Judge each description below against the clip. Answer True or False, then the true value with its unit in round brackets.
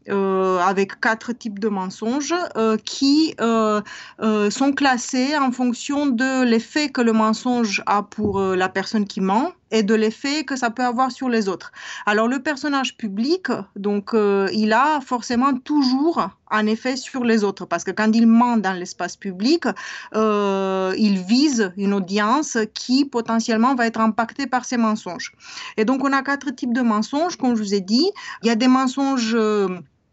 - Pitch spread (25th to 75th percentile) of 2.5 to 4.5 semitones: True (4.0 semitones)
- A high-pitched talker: True (225 Hz)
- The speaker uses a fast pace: False (180 wpm)